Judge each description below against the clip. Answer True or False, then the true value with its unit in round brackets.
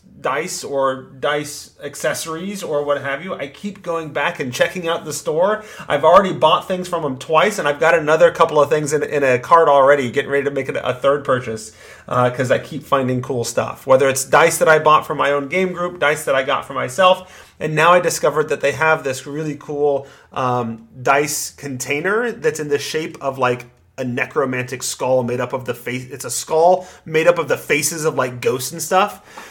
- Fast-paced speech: True (220 wpm)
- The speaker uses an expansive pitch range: False (4.1 semitones)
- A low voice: False (145 Hz)